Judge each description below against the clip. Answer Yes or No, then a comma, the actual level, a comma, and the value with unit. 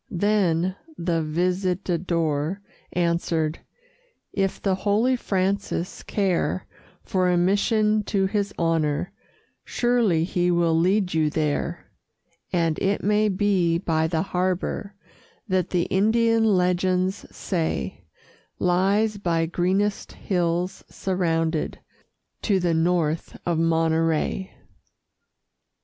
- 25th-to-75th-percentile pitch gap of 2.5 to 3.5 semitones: Yes, average, 3.0 semitones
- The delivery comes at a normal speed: No, slow, 100 wpm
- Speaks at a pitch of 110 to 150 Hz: No, medium, 180 Hz